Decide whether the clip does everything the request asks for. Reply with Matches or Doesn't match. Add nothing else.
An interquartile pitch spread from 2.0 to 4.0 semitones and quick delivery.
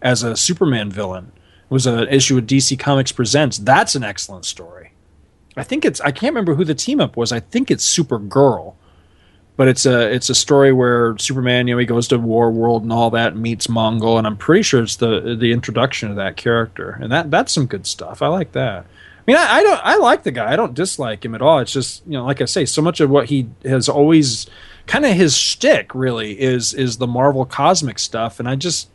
Matches